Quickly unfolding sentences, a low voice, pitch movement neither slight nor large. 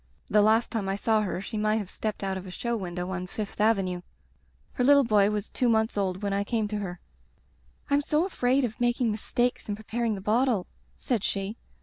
No: fast, 215 wpm; high, 215 Hz; average, 3.3 semitones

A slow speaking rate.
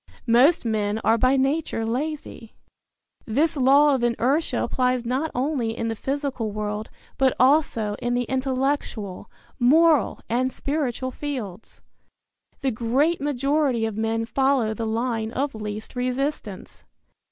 Yes: slow, 130 wpm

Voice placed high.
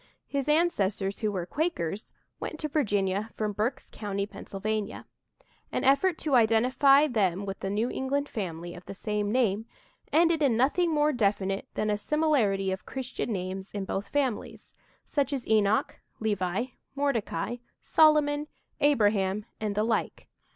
Yes: high, 220 Hz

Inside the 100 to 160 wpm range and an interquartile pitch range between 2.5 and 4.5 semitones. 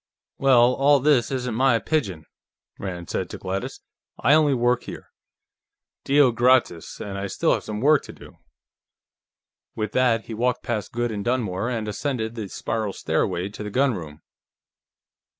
Yes: average, 155 wpm; average, 4.1 semitones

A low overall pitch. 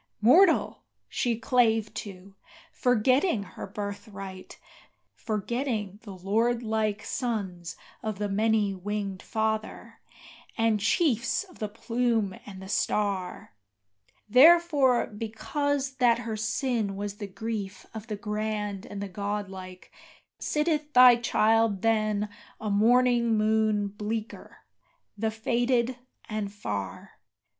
No: high, 215 Hz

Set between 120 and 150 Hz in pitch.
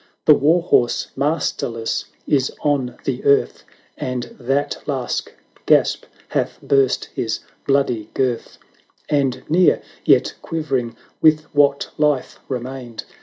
Yes: low, 135 Hz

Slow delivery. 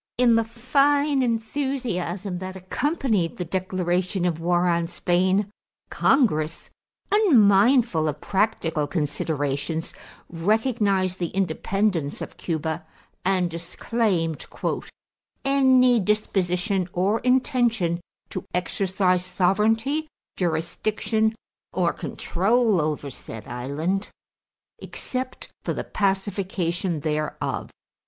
Yes: slow, 90 wpm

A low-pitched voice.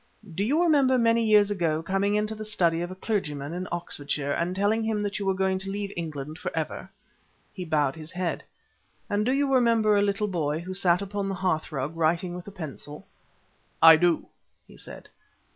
No: high, 190 Hz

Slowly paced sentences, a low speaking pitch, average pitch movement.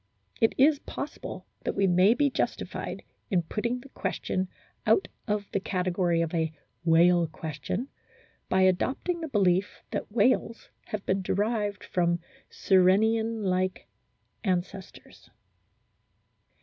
No: slow, 120 wpm; high, 190 Hz; average, 3.8 semitones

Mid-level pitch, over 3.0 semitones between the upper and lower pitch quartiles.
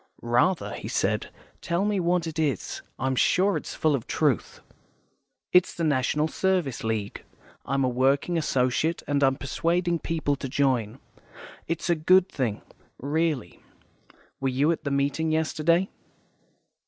Yes: medium, 150 Hz; average, 4.2 semitones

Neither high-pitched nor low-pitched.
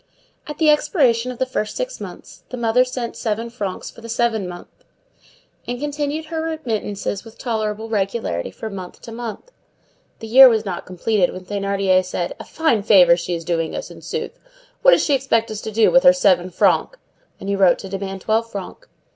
No: high, 220 Hz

